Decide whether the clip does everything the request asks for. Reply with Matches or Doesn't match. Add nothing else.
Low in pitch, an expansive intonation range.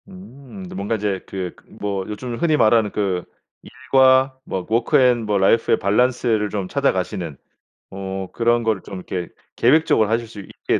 Doesn't match